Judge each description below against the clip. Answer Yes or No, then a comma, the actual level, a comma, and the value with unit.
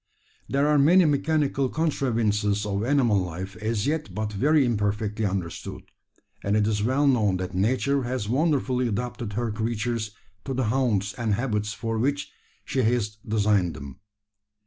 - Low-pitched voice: Yes, low, 115 Hz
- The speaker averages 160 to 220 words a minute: No, average, 150 wpm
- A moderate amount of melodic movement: Yes, average, 4.5 semitones